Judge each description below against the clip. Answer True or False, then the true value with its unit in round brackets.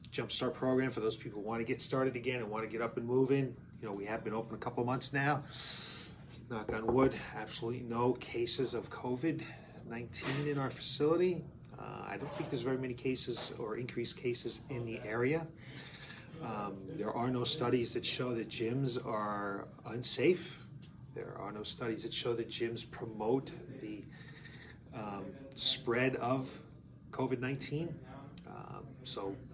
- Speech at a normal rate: True (165 wpm)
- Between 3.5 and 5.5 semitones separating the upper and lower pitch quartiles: False (2.6 semitones)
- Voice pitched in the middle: False (125 Hz)